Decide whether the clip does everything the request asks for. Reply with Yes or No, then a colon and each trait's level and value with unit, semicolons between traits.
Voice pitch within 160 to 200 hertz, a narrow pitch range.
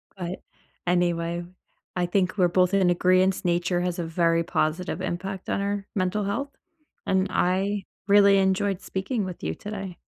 Yes: medium, 185 Hz; narrow, 2.0 semitones